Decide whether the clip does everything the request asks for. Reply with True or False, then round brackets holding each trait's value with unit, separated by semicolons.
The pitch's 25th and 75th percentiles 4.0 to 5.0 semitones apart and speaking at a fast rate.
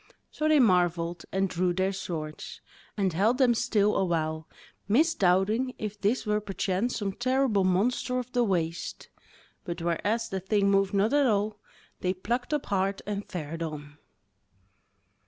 False (4.3 semitones; 150 wpm)